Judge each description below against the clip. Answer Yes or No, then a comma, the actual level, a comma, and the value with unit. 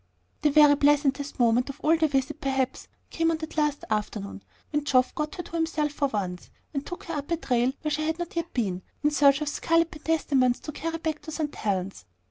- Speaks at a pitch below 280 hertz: No, very high, 295 Hz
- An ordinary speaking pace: No, fast, 215 wpm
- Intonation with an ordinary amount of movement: Yes, average, 3.6 semitones